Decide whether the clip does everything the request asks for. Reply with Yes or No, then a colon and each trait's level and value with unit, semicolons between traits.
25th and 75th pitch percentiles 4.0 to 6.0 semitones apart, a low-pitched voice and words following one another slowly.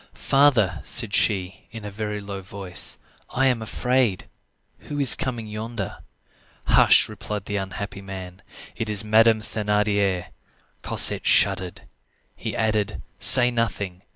No: average, 2.7 semitones; low, 105 Hz; slow, 125 wpm